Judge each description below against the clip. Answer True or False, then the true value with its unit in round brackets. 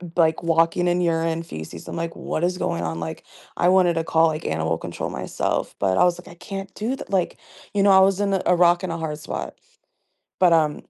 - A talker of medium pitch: True (170 Hz)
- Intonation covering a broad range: False (2.4 semitones)